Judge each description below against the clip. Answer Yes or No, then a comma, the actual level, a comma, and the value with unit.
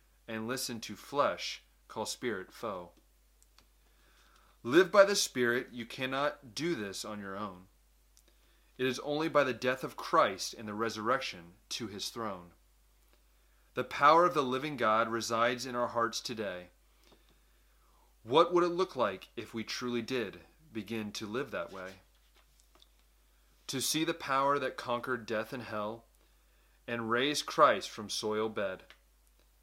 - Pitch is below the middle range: Yes, low, 115 Hz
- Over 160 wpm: No, average, 145 wpm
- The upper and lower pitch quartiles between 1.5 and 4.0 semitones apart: No, average, 4.6 semitones